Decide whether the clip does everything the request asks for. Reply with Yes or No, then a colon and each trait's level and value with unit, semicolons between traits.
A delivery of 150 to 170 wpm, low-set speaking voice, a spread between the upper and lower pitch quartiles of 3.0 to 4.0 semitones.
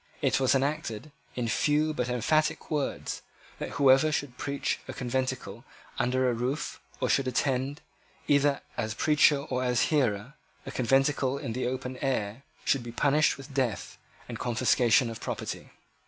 No: average, 155 wpm; low, 130 Hz; narrow, 2.6 semitones